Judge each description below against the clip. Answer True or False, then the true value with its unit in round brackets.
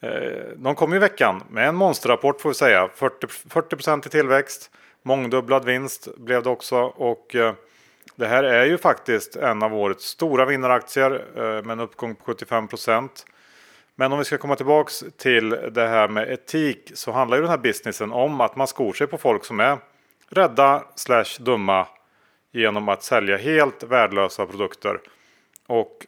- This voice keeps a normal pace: True (170 wpm)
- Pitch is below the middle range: True (130 Hz)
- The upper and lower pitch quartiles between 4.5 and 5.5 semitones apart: False (3.7 semitones)